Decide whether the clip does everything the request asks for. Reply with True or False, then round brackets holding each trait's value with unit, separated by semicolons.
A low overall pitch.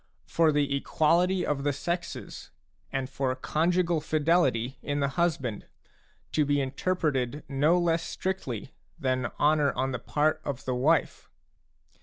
False (145 Hz)